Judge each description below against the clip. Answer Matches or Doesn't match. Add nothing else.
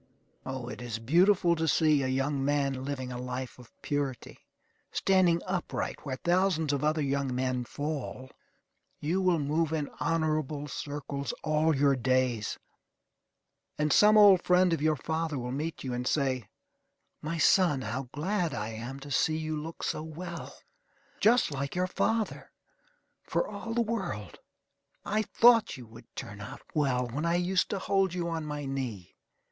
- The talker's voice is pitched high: Doesn't match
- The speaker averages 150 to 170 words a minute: Matches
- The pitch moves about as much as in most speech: Matches